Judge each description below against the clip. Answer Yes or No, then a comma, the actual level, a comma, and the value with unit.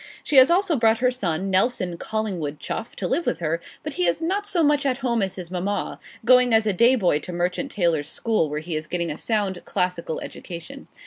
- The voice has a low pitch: No, high, 195 Hz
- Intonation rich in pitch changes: Yes, wide, 6.6 semitones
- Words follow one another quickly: Yes, fast, 220 wpm